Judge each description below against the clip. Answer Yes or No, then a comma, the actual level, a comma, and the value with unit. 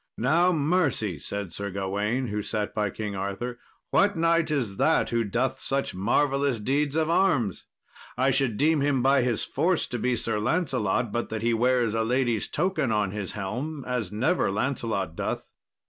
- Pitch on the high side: No, low, 120 Hz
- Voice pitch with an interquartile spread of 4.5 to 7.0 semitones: Yes, average, 5.1 semitones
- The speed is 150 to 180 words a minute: Yes, average, 175 wpm